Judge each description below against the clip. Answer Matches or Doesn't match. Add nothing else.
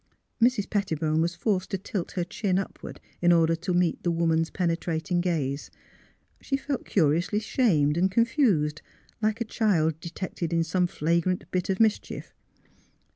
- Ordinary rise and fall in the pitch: Matches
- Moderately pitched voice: Matches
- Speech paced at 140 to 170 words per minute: Matches